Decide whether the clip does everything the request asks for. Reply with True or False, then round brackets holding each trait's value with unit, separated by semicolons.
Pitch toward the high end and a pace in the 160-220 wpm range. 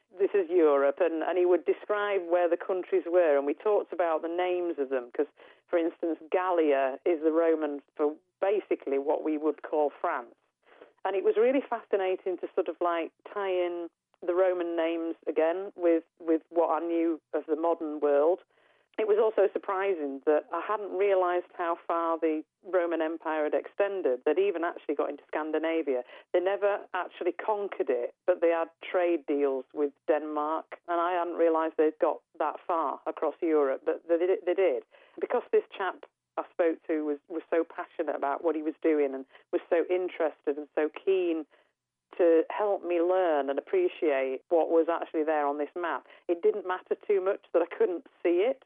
False (170 Hz; 185 wpm)